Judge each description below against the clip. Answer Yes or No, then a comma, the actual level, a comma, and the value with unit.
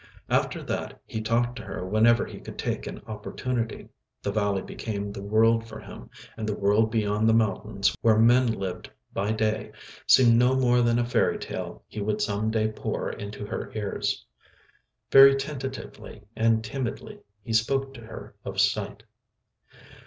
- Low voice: Yes, low, 110 Hz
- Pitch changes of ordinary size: No, narrow, 2.2 semitones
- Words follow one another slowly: No, average, 165 wpm